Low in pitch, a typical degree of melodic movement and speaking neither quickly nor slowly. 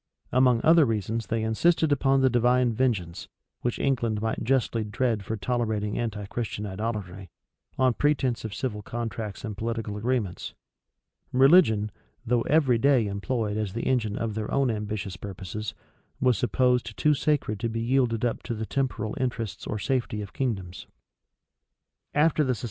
Yes: low, 115 Hz; average, 3.3 semitones; average, 155 wpm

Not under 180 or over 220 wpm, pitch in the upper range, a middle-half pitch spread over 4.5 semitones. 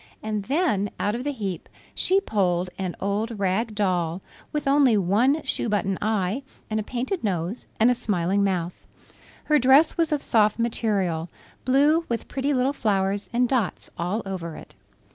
No: average, 165 wpm; high, 215 Hz; average, 5.1 semitones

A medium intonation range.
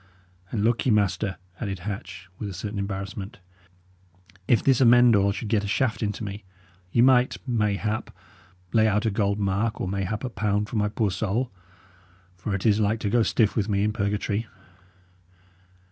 No: narrow, 2.1 semitones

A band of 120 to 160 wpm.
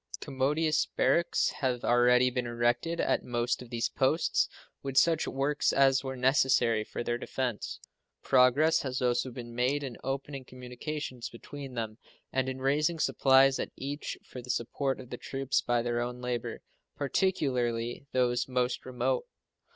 Yes: average, 150 wpm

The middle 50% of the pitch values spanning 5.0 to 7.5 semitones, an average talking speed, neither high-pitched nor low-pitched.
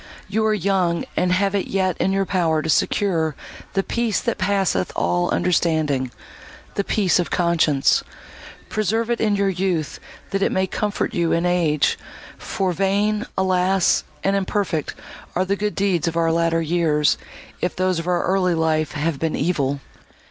No: average, 3.2 semitones; average, 160 wpm; medium, 180 Hz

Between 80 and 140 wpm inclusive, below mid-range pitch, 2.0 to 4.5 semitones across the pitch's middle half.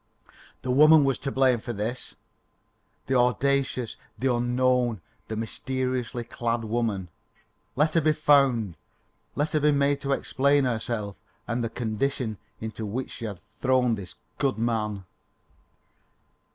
Yes: slow, 135 wpm; low, 125 Hz; average, 3.4 semitones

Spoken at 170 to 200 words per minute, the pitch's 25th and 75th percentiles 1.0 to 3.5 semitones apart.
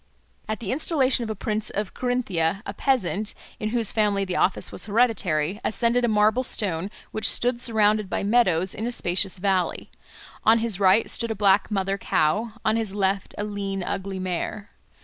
Yes: average, 180 wpm; average, 2.8 semitones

